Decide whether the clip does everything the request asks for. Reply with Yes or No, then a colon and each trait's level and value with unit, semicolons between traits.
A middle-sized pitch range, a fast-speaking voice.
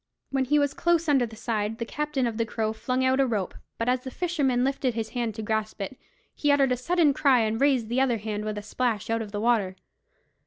Yes: average, 3.7 semitones; fast, 245 wpm